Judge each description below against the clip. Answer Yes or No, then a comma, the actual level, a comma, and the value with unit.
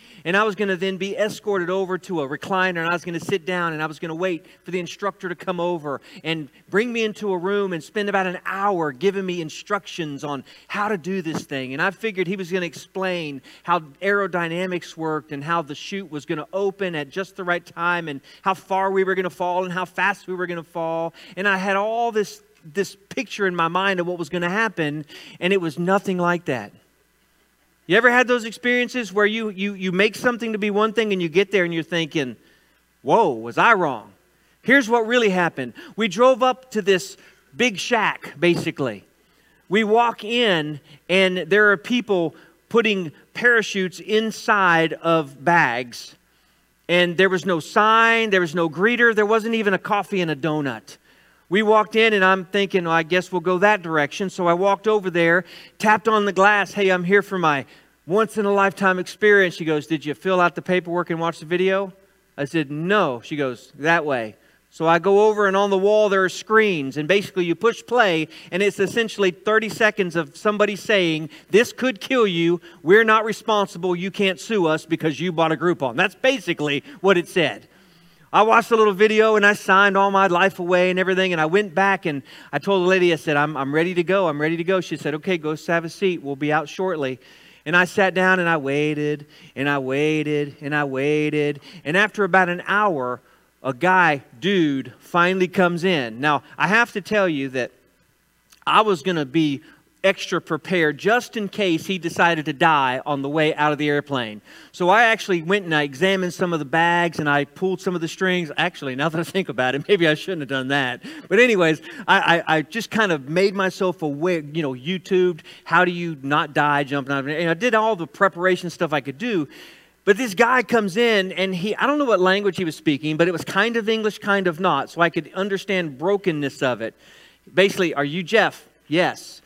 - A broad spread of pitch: No, average, 4.0 semitones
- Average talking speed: No, fast, 220 wpm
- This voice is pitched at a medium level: Yes, medium, 180 Hz